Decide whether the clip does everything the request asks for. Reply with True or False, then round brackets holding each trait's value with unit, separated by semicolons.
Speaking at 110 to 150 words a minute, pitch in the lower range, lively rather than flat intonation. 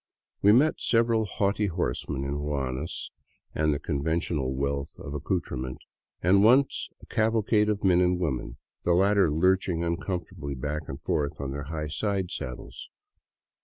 True (145 wpm; 85 Hz; 5.8 semitones)